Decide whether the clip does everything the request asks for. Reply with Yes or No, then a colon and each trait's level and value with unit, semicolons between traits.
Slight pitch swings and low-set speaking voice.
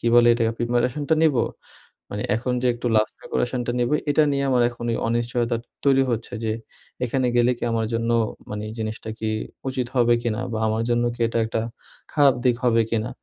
Yes: narrow, 1.6 semitones; low, 120 Hz